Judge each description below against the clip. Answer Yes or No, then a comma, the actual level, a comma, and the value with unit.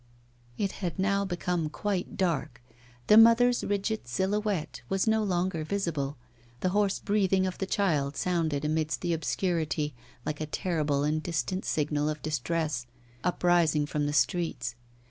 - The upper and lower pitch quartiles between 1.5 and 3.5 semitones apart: No, average, 4.2 semitones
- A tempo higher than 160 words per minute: No, average, 145 wpm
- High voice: No, medium, 170 Hz